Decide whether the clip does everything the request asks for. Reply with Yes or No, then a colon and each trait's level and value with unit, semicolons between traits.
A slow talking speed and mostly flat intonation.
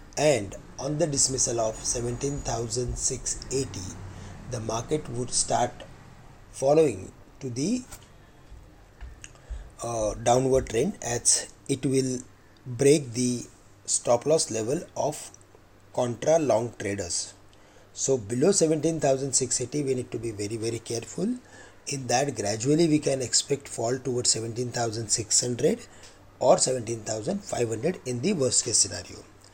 No: slow, 110 wpm; average, 4.3 semitones